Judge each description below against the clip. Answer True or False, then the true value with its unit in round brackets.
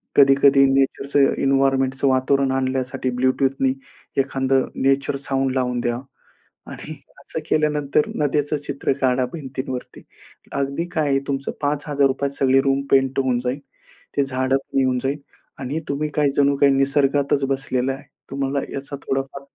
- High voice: False (135 Hz)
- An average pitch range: False (1.0 semitones)